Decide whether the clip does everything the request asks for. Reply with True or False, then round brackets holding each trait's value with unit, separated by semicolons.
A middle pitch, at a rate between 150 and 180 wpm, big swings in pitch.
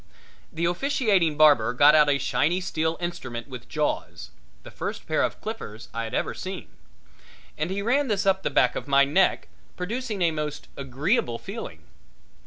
True (160 Hz; 170 wpm; 5.8 semitones)